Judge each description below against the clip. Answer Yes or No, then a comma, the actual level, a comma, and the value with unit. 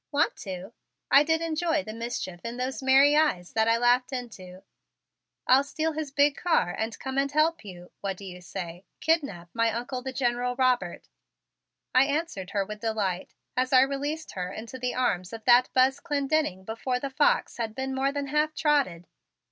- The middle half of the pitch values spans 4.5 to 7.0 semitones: Yes, average, 5.1 semitones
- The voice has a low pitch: No, very high, 250 Hz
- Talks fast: No, average, 185 wpm